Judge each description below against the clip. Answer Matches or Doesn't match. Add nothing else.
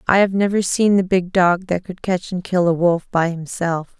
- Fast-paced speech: Matches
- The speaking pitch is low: Doesn't match